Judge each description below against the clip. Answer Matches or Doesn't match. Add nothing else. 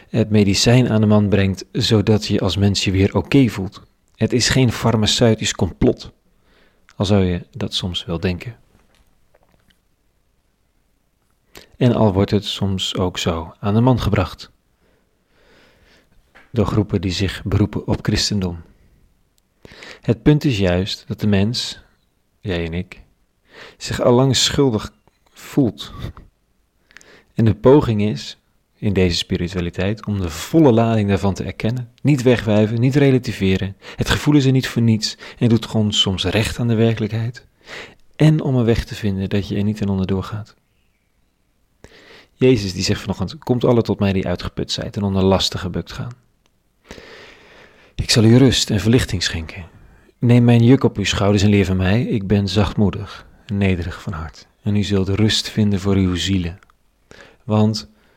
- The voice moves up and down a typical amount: Matches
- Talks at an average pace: Matches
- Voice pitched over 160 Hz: Doesn't match